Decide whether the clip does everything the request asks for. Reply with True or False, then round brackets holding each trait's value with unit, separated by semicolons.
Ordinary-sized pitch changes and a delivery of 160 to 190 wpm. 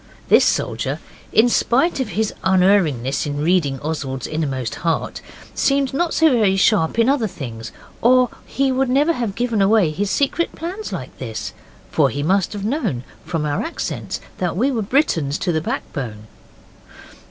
False (9.0 semitones; 165 wpm)